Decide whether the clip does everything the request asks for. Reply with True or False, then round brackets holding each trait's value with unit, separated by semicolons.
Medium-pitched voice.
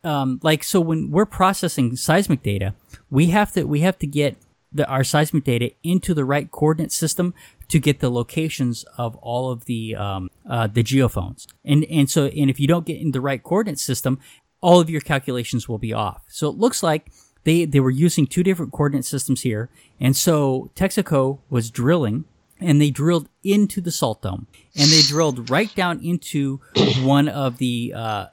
True (145 Hz)